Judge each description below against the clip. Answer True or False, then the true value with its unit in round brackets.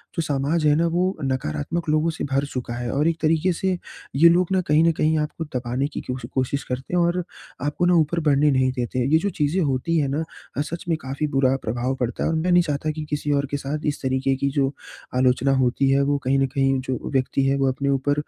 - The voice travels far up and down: False (3.2 semitones)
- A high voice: False (140 Hz)